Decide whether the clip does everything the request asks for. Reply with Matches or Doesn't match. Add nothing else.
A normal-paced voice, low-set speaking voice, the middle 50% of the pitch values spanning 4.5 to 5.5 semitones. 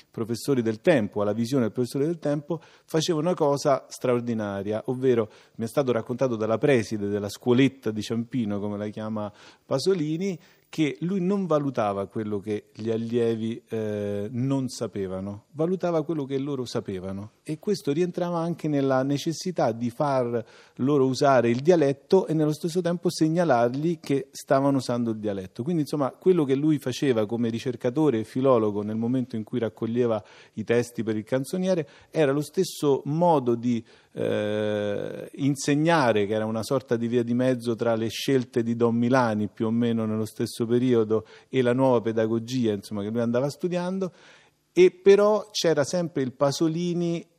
Matches